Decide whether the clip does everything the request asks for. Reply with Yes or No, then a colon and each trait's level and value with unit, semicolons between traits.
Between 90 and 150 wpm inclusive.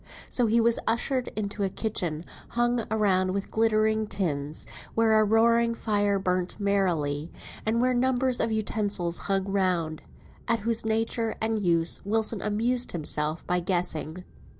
Yes: average, 145 wpm